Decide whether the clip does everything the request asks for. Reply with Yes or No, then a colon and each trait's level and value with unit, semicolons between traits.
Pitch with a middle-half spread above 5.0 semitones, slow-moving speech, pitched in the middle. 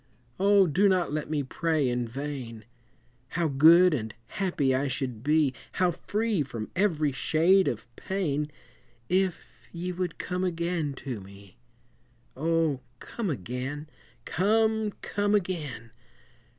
Yes: wide, 5.5 semitones; slow, 125 wpm; medium, 155 Hz